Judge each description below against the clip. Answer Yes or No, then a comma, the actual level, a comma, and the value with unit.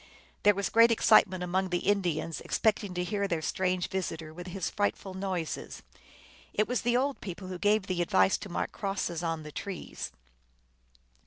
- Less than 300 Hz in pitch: Yes, high, 190 Hz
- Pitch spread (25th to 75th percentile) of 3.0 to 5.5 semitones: No, narrow, 2.6 semitones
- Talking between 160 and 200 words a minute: Yes, average, 180 wpm